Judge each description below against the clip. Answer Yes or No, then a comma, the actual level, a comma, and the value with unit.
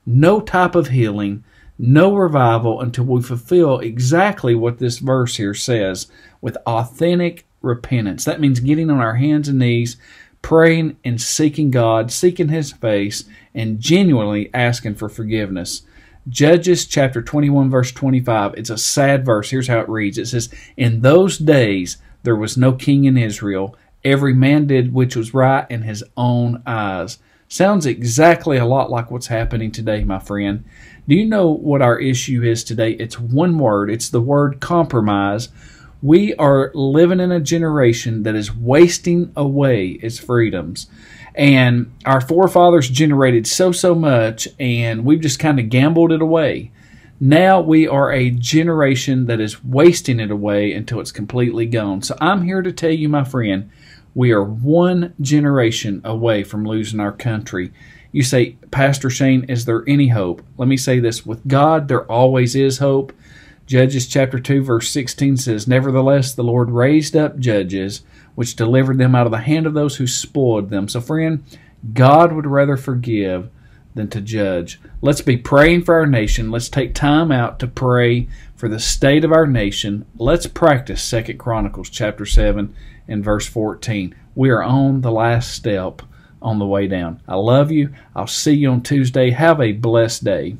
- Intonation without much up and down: No, average, 4.3 semitones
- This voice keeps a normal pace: Yes, average, 170 wpm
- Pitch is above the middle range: No, low, 125 Hz